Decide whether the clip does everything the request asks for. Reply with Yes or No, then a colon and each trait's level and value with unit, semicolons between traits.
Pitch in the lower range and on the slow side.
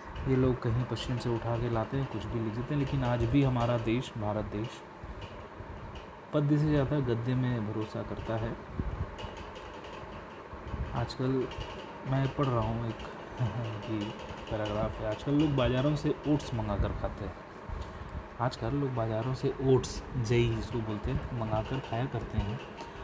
No: low, 115 Hz; average, 155 wpm